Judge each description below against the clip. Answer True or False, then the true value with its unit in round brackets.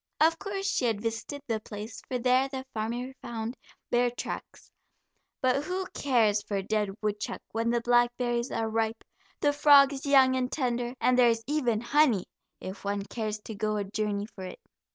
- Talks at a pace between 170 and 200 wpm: True (180 wpm)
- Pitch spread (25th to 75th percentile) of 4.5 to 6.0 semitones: False (3.3 semitones)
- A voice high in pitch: True (240 Hz)